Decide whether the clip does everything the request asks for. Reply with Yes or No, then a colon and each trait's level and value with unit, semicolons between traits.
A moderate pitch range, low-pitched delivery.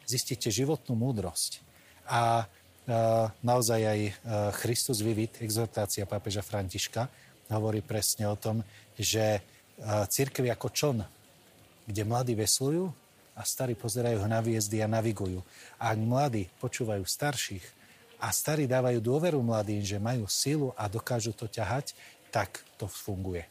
Yes: average, 3.0 semitones; low, 115 Hz